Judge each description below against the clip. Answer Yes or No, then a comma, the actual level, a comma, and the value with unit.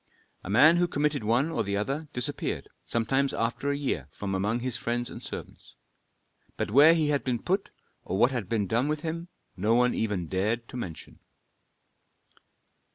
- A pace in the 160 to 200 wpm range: Yes, average, 175 wpm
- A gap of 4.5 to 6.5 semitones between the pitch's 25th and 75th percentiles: Yes, wide, 5.5 semitones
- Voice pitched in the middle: No, low, 120 Hz